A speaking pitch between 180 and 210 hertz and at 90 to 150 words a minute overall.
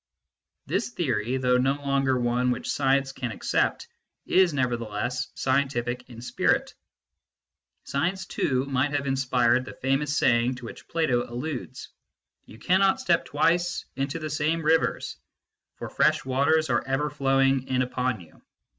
No: low, 135 Hz; average, 145 wpm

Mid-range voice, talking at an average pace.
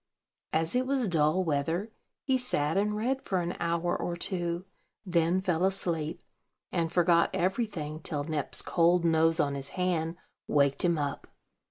Yes: medium, 170 Hz; average, 155 wpm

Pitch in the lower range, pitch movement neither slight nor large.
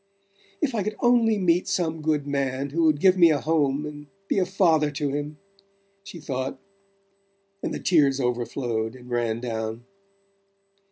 No: medium, 145 Hz; average, 4.5 semitones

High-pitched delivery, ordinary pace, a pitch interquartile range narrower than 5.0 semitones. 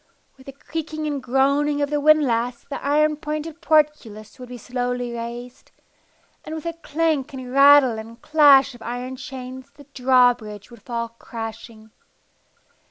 Yes: very high, 260 Hz; average, 150 wpm; average, 3.5 semitones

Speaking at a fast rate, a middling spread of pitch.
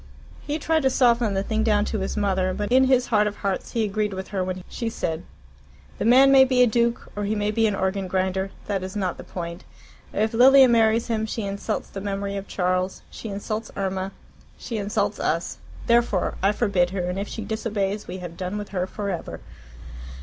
Yes: fast, 215 wpm; average, 3.0 semitones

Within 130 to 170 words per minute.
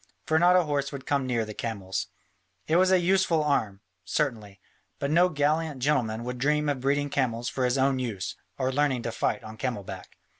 No: average, 200 wpm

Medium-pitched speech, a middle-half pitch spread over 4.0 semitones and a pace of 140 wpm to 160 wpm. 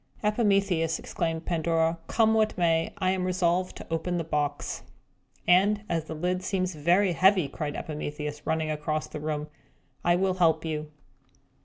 No: medium, 170 Hz; average, 3.0 semitones; average, 155 wpm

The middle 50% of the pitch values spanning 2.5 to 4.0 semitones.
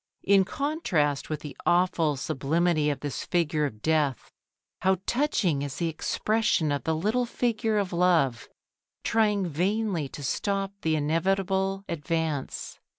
No: average, 4.7 semitones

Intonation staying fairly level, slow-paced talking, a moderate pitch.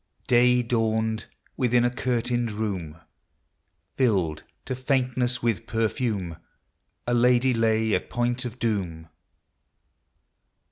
No: narrow, 2.2 semitones; slow, 105 wpm; low, 120 Hz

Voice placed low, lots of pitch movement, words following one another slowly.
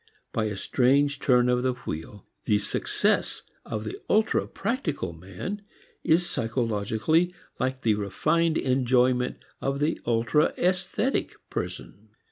Yes: low, 125 Hz; wide, 6.3 semitones; slow, 120 wpm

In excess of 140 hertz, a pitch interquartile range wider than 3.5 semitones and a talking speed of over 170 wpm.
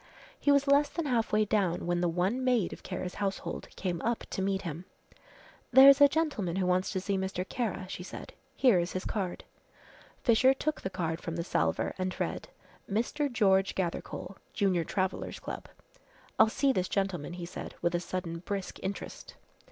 Yes: high, 190 Hz; average, 4.6 semitones; average, 185 wpm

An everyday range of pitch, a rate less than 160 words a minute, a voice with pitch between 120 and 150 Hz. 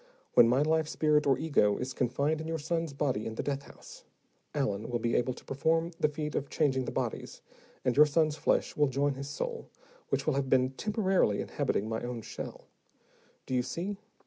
No: average, 3.7 semitones; average, 200 wpm; medium, 140 Hz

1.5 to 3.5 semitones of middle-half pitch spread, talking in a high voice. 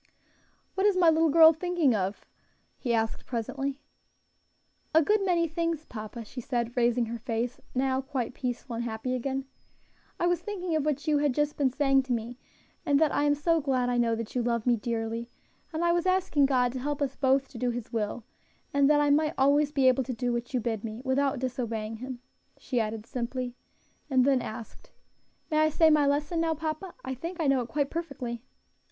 No: average, 4.1 semitones; very high, 265 Hz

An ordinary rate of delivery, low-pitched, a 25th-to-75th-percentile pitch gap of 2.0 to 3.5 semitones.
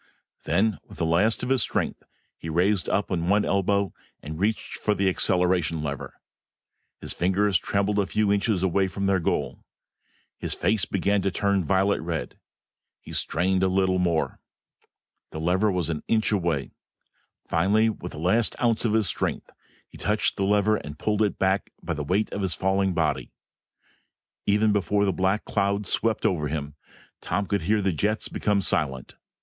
Yes: average, 175 wpm; very low, 95 Hz; average, 2.9 semitones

